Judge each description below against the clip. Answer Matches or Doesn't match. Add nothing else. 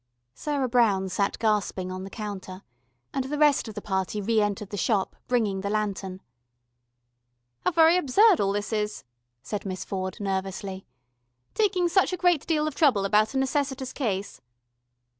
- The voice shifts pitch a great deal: Matches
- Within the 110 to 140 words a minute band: Doesn't match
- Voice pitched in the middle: Doesn't match